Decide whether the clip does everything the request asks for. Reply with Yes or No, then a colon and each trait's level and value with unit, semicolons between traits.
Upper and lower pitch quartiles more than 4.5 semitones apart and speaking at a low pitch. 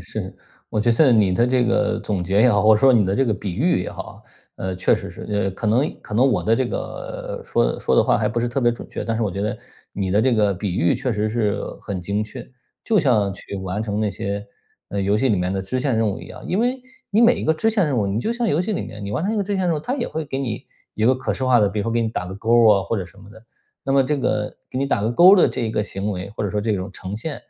Yes: average, 4.9 semitones; low, 110 Hz